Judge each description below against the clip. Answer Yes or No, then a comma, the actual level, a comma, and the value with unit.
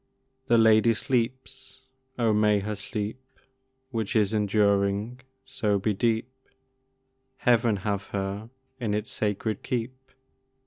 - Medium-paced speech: No, slow, 115 wpm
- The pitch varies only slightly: Yes, narrow, 2.3 semitones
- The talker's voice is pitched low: Yes, low, 110 Hz